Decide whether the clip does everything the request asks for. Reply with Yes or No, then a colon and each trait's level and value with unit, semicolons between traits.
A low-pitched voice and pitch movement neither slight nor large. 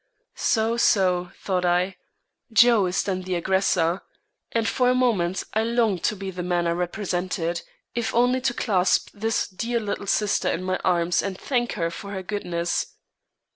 No: high, 190 Hz; average, 4.0 semitones